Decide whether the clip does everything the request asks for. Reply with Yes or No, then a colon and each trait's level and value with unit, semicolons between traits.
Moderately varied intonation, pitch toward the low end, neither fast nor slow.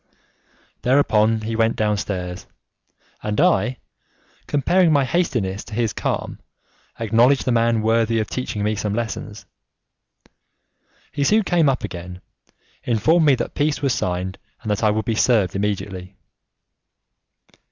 No: average, 4.0 semitones; low, 115 Hz; slow, 130 wpm